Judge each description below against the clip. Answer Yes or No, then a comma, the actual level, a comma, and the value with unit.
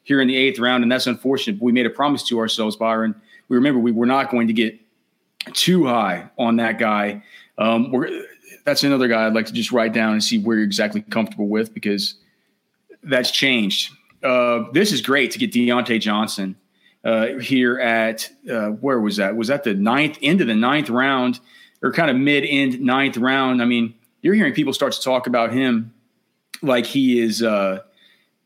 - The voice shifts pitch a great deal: No, average, 2.8 semitones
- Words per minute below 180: No, average, 195 wpm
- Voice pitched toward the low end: Yes, low, 120 Hz